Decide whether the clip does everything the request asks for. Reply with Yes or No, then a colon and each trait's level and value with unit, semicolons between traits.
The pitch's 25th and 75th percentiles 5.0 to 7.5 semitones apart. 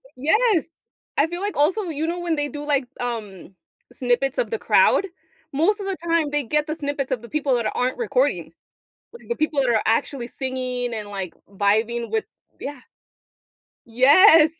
Yes: wide, 5.4 semitones